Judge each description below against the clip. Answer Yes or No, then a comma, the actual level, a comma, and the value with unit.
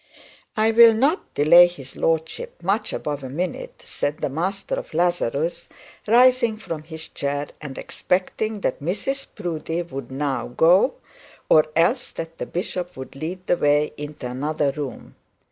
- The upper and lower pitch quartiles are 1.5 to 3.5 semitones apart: No, average, 4.6 semitones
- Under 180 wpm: Yes, average, 150 wpm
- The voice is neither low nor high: Yes, medium, 165 Hz